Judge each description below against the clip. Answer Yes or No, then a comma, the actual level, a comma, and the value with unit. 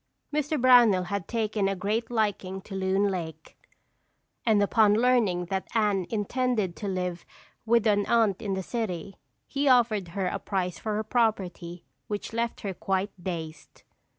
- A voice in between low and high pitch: No, high, 205 Hz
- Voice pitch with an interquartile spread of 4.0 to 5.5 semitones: No, average, 3.4 semitones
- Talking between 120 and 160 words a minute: Yes, average, 155 wpm